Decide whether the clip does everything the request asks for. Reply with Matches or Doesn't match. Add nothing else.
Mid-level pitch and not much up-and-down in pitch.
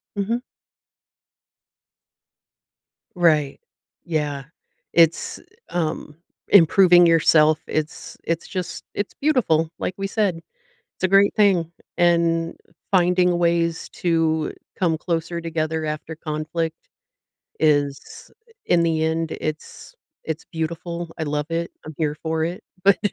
Matches